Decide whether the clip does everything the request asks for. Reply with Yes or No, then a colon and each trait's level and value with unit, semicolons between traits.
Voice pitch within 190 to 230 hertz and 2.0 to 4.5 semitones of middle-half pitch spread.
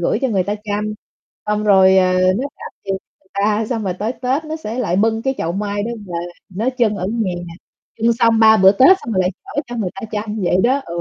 Yes: high, 210 Hz; average, 3.3 semitones